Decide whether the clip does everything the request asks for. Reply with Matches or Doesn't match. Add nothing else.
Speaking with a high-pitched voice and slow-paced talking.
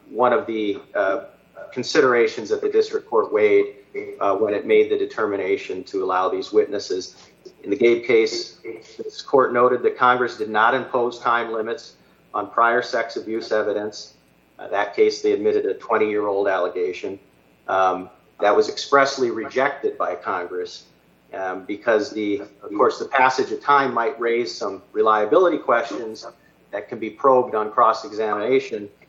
Doesn't match